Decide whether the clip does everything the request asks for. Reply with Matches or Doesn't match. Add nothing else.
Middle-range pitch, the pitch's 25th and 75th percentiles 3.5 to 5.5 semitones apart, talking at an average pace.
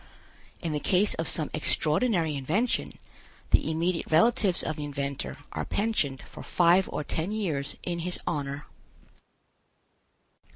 Doesn't match